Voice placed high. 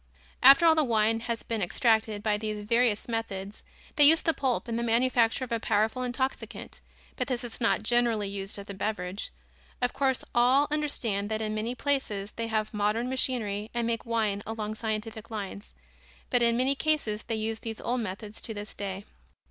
Yes: high, 225 Hz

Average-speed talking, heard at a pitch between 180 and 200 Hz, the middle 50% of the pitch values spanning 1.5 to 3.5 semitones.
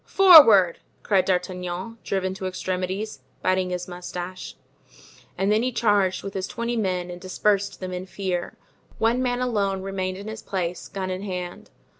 Yes: average, 160 wpm; high, 190 Hz; narrow, 2.5 semitones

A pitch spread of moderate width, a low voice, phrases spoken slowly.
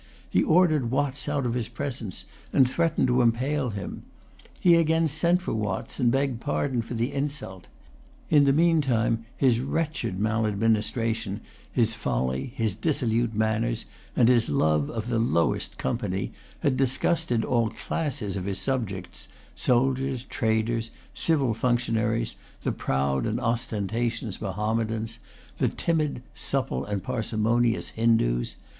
Yes: average, 3.7 semitones; low, 115 Hz; slow, 130 wpm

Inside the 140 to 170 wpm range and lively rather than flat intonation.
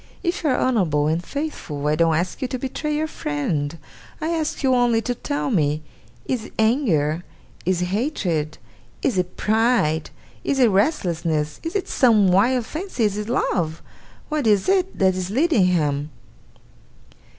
Yes: average, 165 wpm; wide, 8.2 semitones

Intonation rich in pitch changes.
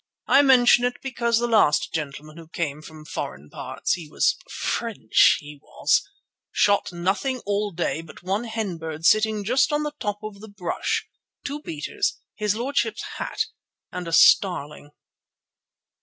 Yes: wide, 6.5 semitones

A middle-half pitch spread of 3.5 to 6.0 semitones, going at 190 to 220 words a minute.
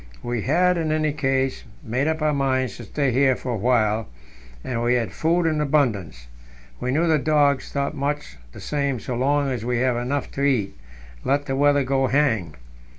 No: average, 3.1 semitones; average, 195 wpm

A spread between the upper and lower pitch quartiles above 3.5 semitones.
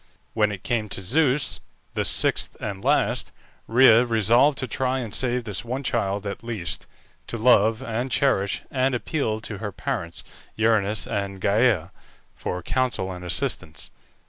Yes: average, 4.1 semitones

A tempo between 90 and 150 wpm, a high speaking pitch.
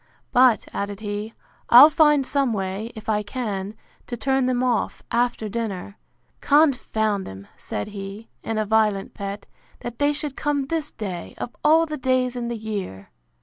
No: average, 160 wpm; high, 225 Hz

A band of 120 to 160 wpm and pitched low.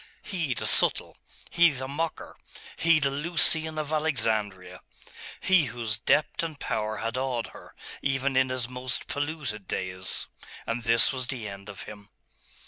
Yes: average, 150 wpm; low, 130 Hz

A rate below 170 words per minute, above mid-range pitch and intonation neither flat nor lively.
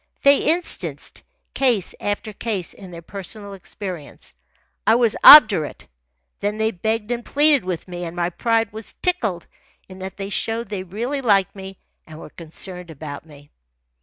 Yes: average, 160 wpm; high, 200 Hz; average, 4.3 semitones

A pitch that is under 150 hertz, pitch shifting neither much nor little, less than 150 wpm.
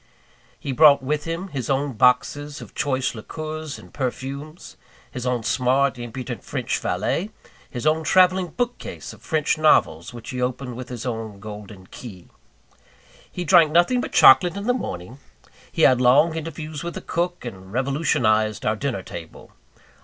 No: low, 135 Hz; average, 4.6 semitones; average, 160 wpm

